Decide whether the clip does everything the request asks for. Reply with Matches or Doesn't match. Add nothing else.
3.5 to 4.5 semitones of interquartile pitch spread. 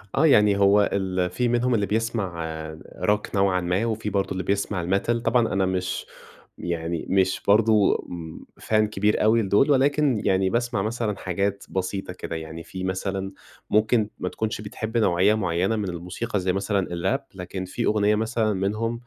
Doesn't match